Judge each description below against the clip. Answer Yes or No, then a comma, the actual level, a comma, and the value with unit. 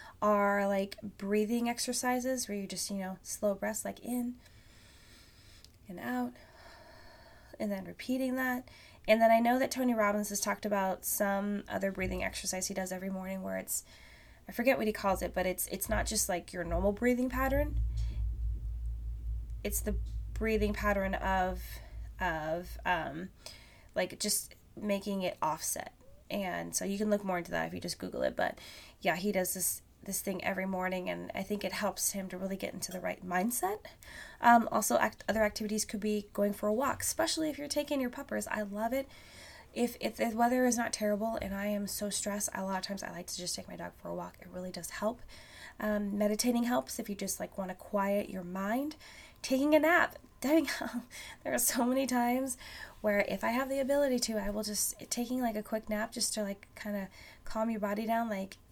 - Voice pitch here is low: No, high, 205 Hz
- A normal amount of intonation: Yes, average, 3.9 semitones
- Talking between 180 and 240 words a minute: Yes, average, 200 wpm